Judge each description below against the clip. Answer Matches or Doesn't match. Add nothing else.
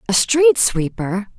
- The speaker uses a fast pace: Doesn't match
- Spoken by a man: Doesn't match